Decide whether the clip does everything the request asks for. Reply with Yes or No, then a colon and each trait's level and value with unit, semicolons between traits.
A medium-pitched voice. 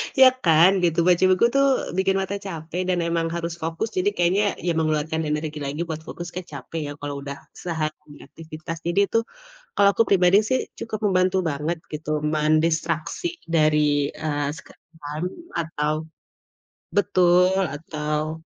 Yes: medium, 165 Hz